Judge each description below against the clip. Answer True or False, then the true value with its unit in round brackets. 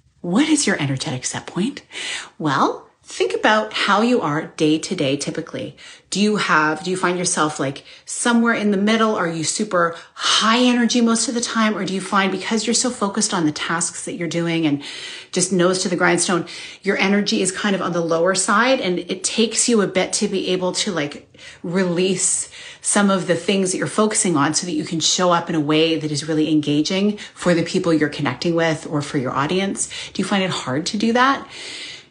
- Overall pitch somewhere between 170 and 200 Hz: True (185 Hz)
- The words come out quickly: True (220 wpm)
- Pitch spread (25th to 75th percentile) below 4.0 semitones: False (4.5 semitones)